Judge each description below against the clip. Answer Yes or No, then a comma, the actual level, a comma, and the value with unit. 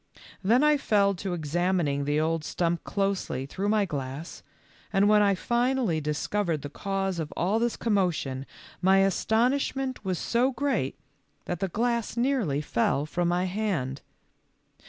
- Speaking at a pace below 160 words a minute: Yes, average, 150 wpm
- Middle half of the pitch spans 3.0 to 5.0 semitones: No, wide, 5.6 semitones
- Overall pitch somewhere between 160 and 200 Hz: Yes, high, 190 Hz